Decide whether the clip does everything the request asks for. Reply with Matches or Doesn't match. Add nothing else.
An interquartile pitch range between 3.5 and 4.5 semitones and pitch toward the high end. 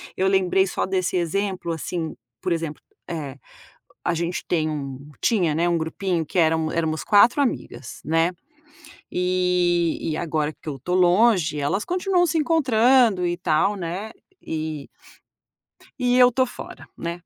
Doesn't match